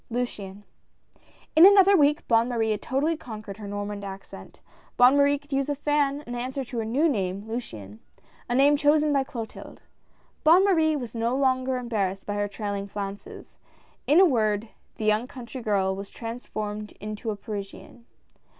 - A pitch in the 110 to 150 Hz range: No, high, 235 Hz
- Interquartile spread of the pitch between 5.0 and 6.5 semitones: Yes, average, 5.3 semitones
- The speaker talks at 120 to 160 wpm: No, average, 170 wpm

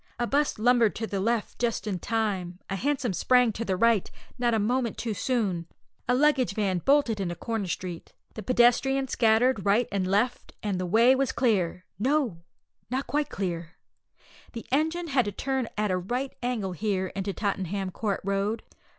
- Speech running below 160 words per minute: No, average, 175 wpm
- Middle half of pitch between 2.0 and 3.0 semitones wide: No, average, 4.4 semitones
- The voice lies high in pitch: Yes, high, 220 Hz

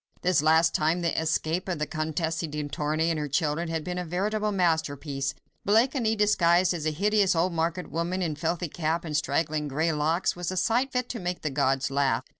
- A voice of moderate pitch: Yes, medium, 165 Hz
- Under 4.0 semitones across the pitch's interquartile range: Yes, average, 3.0 semitones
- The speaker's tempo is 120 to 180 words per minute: No, average, 200 wpm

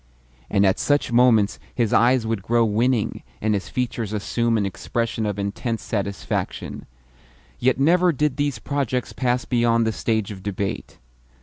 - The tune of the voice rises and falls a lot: No, average, 3.3 semitones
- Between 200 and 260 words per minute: No, average, 150 wpm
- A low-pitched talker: Yes, low, 115 Hz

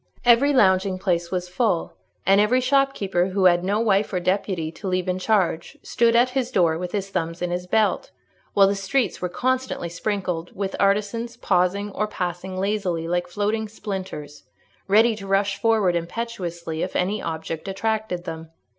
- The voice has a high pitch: Yes, high, 195 Hz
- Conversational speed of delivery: Yes, average, 170 wpm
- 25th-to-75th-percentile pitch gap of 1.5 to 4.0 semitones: Yes, average, 3.4 semitones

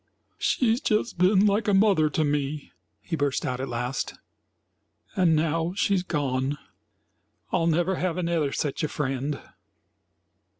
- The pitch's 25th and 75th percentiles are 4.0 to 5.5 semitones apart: Yes, average, 4.4 semitones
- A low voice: No, medium, 160 Hz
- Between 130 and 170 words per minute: Yes, slow, 135 wpm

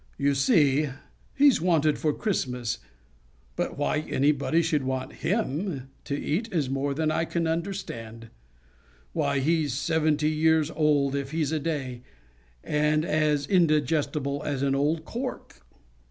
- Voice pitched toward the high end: No, medium, 150 Hz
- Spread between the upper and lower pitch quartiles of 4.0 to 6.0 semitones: No, narrow, 2.6 semitones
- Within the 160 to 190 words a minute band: No, slow, 135 wpm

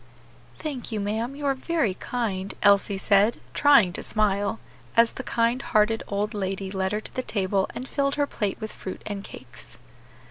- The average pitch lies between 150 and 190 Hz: No, high, 210 Hz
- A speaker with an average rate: Yes, average, 180 wpm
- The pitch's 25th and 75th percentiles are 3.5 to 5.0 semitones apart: Yes, average, 3.8 semitones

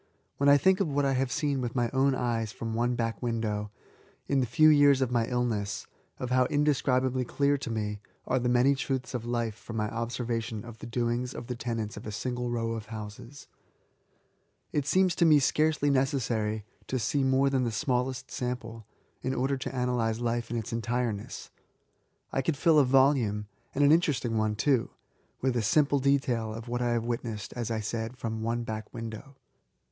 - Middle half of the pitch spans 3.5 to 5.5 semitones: No, average, 2.8 semitones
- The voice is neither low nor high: No, low, 120 Hz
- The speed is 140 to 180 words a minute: No, average, 200 wpm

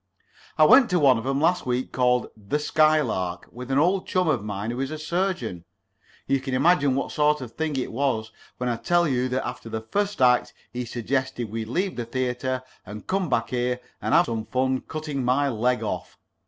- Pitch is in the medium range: No, low, 130 Hz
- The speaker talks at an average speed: No, fast, 210 wpm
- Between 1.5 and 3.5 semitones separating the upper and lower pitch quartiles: No, average, 3.9 semitones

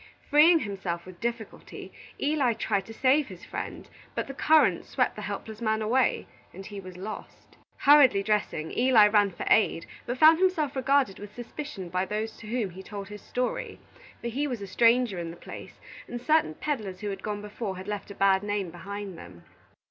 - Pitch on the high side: Yes, high, 210 Hz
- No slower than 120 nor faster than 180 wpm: No, average, 195 wpm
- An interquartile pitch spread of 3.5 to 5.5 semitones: Yes, average, 4.6 semitones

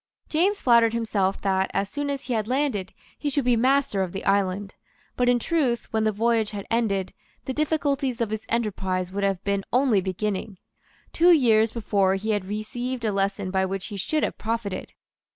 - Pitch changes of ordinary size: Yes, average, 4.1 semitones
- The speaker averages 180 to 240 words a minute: Yes, average, 190 wpm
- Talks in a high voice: Yes, high, 220 Hz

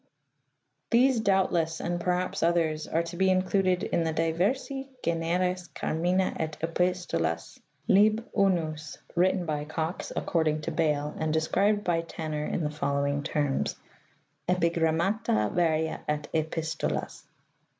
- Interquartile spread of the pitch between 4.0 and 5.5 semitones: No, average, 2.8 semitones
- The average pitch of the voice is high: No, medium, 165 Hz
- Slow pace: Yes, slow, 125 wpm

